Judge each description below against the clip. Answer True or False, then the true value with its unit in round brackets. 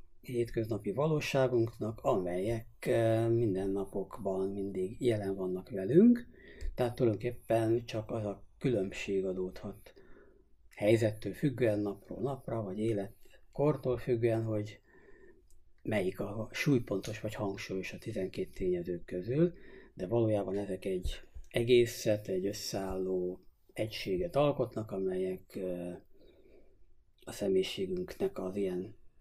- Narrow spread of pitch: False (4.1 semitones)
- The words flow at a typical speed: False (95 wpm)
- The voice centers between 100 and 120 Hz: True (110 Hz)